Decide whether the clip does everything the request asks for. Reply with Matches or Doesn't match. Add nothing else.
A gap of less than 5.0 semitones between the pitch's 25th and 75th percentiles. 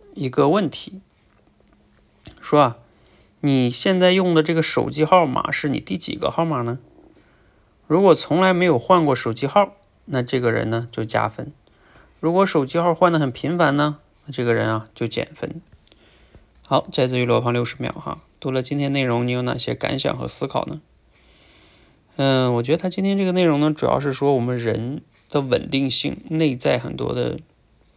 Doesn't match